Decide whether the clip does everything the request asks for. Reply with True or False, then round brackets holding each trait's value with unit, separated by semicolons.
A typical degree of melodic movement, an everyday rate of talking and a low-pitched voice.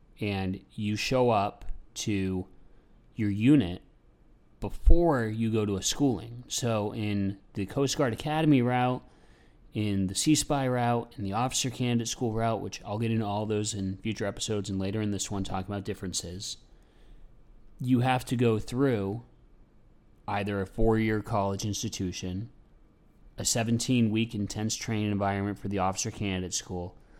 True (3.2 semitones; 150 wpm; 110 Hz)